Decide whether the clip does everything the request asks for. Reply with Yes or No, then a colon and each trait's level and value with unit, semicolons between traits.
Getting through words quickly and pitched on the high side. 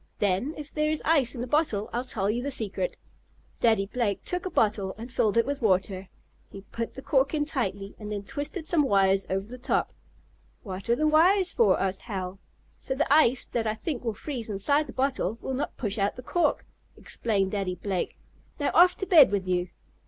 Yes: fast, 210 wpm; high, 235 Hz